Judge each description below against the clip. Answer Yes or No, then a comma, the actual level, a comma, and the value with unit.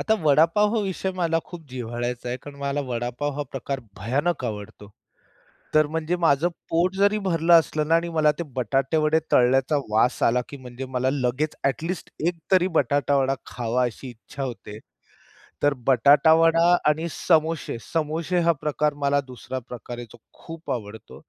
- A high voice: No, medium, 145 Hz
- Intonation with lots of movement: No, average, 4.7 semitones